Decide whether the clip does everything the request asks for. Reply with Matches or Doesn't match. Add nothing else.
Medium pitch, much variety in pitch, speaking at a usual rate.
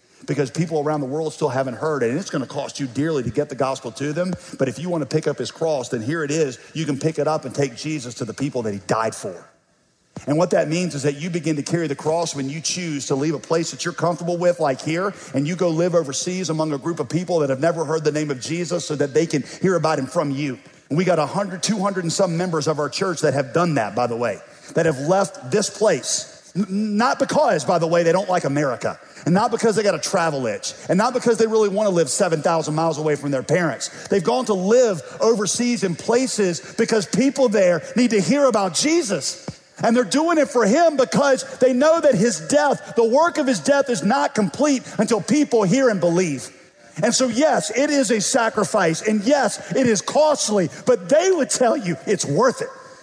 Doesn't match